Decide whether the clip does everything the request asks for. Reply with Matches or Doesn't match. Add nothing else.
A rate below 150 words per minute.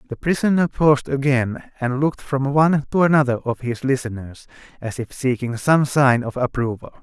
Doesn't match